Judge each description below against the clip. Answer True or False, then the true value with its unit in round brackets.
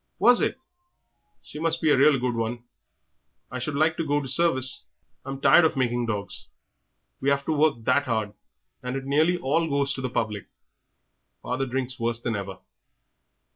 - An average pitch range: True (3.9 semitones)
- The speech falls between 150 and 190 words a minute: True (175 wpm)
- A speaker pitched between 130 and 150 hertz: True (135 Hz)